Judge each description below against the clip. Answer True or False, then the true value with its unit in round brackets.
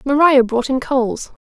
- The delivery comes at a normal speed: True (170 wpm)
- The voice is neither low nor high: False (265 Hz)